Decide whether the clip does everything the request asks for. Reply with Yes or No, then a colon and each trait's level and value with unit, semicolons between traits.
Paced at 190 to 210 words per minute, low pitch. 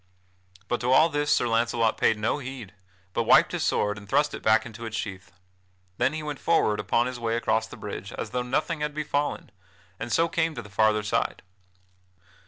Yes: average, 200 wpm; low, 120 Hz